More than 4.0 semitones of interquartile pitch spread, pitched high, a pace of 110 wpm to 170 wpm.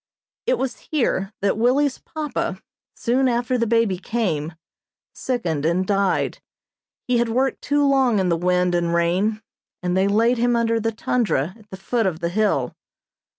Yes: average, 5.1 semitones; high, 220 Hz; average, 165 wpm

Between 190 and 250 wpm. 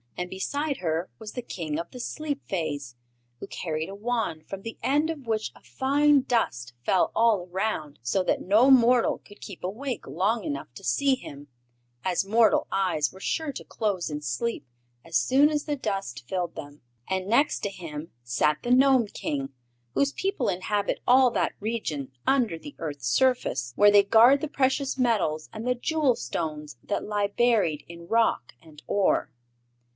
No: average, 175 wpm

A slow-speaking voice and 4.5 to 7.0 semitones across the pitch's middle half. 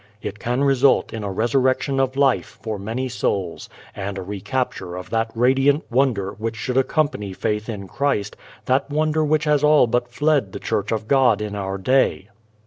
No: average, 180 wpm; average, 4.8 semitones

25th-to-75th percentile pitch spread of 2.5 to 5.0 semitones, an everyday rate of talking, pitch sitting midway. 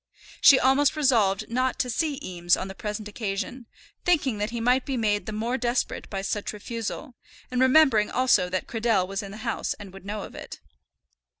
No: average, 4.1 semitones; average, 195 wpm; high, 225 Hz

